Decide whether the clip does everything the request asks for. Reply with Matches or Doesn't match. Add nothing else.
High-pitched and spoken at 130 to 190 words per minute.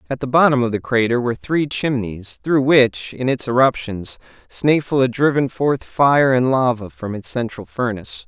Doesn't match